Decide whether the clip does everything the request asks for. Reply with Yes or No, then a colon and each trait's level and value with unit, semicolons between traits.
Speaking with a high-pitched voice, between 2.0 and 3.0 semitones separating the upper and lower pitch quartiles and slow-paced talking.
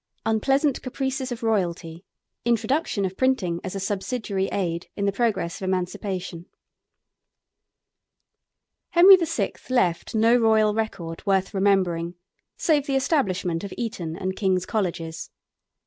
No: high, 200 Hz; average, 4.9 semitones; slow, 120 wpm